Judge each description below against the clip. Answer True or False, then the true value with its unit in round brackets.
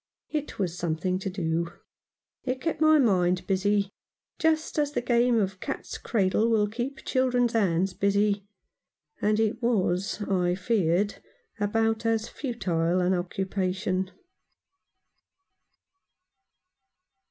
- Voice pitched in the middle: False (205 Hz)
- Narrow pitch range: False (4.2 semitones)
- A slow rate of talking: True (110 wpm)